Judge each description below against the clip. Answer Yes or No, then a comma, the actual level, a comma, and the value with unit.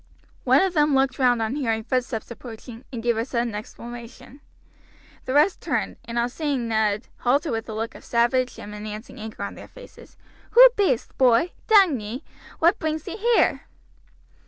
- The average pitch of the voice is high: Yes, high, 245 Hz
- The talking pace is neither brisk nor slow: Yes, average, 175 wpm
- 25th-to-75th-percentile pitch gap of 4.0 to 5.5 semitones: Yes, average, 4.4 semitones